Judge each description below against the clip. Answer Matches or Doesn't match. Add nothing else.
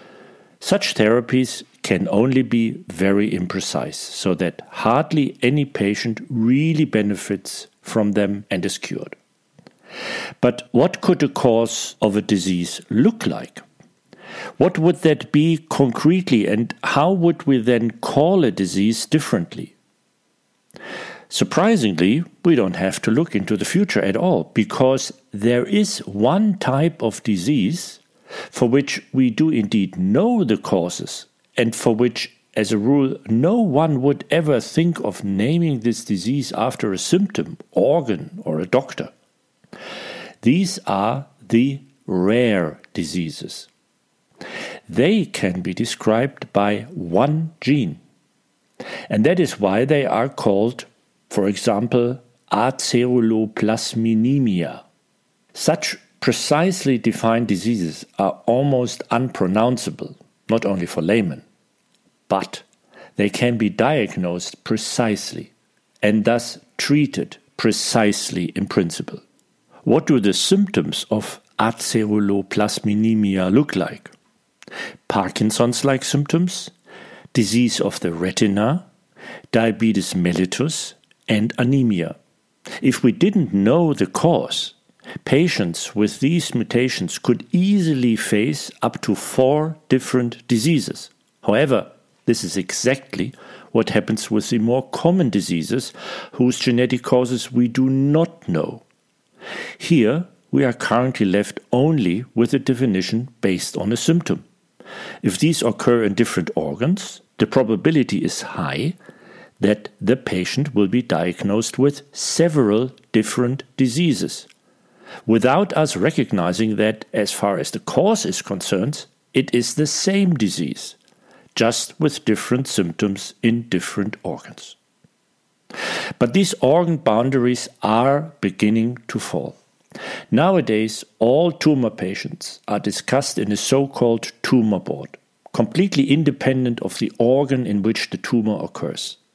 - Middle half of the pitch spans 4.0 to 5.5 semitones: Matches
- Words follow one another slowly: Matches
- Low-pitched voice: Matches